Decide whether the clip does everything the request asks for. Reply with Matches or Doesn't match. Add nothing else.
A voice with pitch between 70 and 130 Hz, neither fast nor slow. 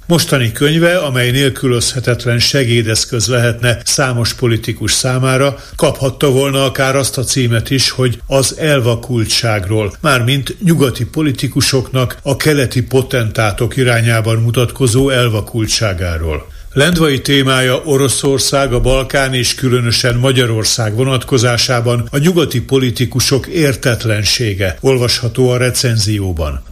Doesn't match